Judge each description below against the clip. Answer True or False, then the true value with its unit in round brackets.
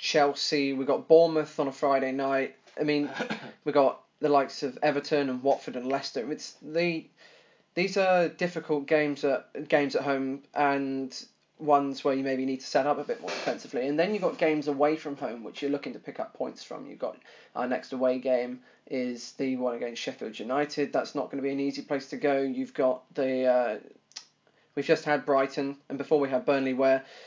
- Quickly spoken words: True (210 wpm)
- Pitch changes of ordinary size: False (2.0 semitones)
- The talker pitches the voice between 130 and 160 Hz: True (140 Hz)